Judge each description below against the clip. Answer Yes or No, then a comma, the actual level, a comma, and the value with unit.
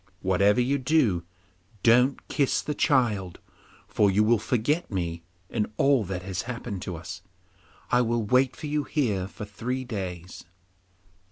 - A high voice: No, low, 115 Hz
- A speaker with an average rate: Yes, average, 150 wpm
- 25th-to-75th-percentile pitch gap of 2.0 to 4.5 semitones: No, average, 5.2 semitones